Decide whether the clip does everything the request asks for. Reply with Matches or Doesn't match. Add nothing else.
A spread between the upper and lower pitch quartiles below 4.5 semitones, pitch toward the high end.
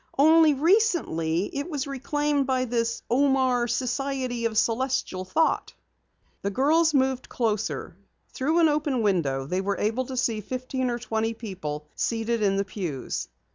Doesn't match